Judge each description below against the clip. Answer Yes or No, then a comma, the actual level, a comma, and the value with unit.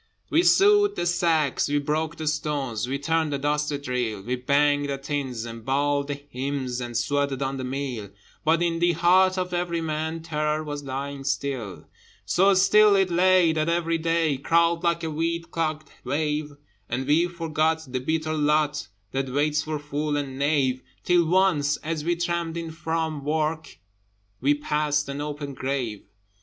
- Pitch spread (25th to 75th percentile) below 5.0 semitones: Yes, average, 3.0 semitones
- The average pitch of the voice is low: No, medium, 150 Hz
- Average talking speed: Yes, average, 170 wpm